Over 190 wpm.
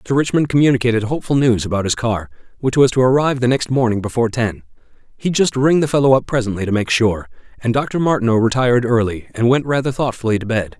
Yes: average, 200 wpm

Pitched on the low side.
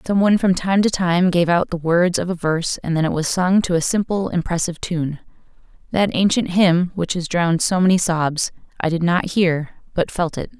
No: medium, 175 Hz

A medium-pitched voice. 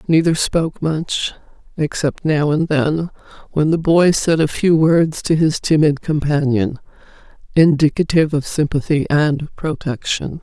Yes: medium, 155 Hz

